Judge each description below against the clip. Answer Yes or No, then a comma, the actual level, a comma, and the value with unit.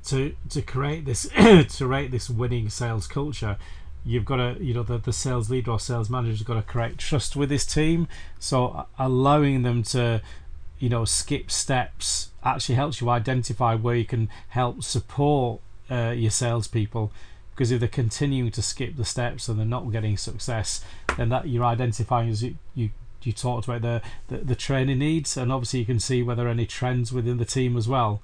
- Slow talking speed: No, average, 195 wpm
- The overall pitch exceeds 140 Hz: No, low, 120 Hz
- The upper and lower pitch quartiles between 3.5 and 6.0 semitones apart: No, narrow, 2.4 semitones